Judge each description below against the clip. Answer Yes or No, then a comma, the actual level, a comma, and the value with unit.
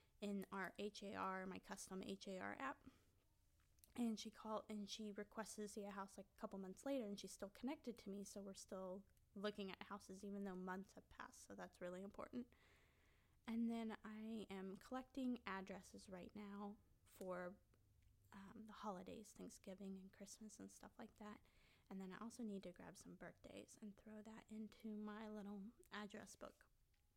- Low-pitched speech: No, high, 205 Hz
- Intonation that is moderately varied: No, narrow, 2.2 semitones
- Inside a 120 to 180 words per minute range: Yes, average, 175 wpm